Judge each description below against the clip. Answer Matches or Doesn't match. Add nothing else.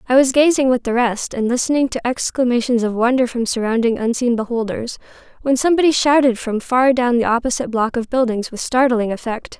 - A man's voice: Doesn't match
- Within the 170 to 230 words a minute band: Matches